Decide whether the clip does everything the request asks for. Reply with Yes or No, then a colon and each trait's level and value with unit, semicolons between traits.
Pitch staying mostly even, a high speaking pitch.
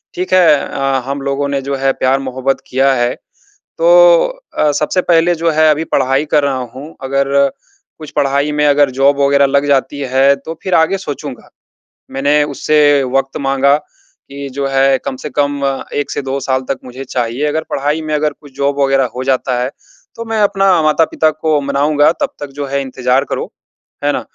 No: narrow, 1.9 semitones; medium, 140 Hz